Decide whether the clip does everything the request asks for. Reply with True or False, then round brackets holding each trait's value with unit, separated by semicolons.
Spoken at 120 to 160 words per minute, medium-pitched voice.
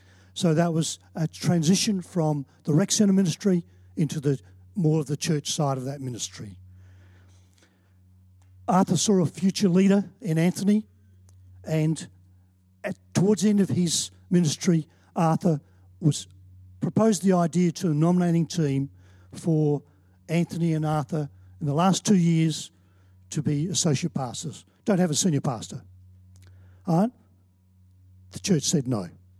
True (135 wpm; 150 Hz)